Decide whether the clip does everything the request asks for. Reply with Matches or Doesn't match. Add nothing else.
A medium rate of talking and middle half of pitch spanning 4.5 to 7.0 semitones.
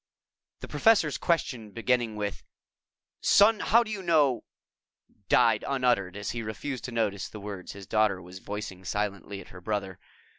Matches